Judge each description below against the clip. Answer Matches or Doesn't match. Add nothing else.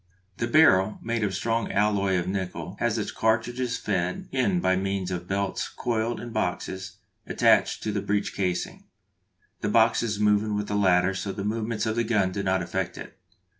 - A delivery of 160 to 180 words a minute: Doesn't match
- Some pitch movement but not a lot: Matches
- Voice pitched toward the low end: Matches